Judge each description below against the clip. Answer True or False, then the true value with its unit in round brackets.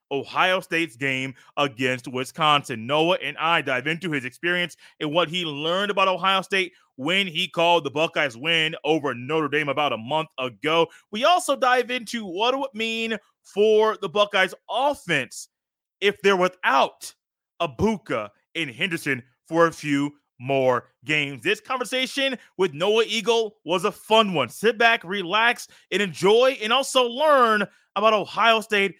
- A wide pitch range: True (6.2 semitones)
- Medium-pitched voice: True (180 Hz)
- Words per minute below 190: True (160 wpm)